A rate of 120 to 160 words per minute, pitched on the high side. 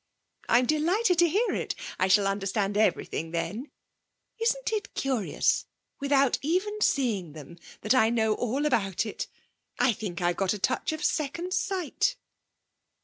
Yes: average, 145 wpm; high, 245 Hz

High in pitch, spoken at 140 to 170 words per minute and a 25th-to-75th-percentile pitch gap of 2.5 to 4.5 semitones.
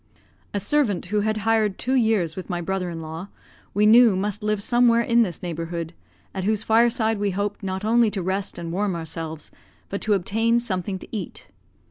No: high, 205 Hz; average, 190 wpm; average, 3.5 semitones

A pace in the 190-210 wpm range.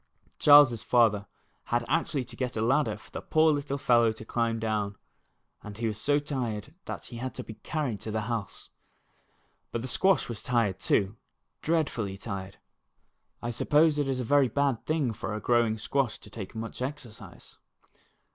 No: average, 175 wpm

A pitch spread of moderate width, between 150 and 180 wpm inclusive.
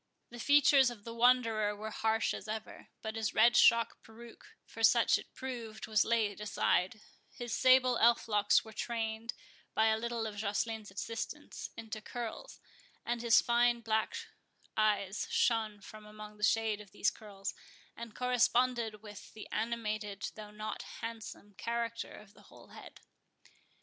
No: narrow, 1.8 semitones; average, 155 wpm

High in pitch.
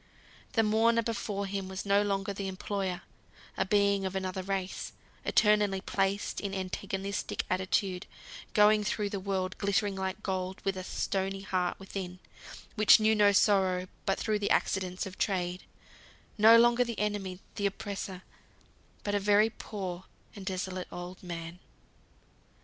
Yes: high, 195 Hz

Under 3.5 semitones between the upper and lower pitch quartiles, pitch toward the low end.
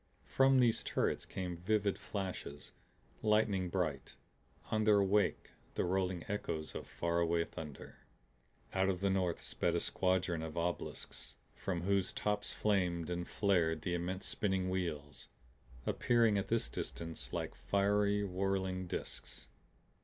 Yes: average, 2.8 semitones; very low, 95 Hz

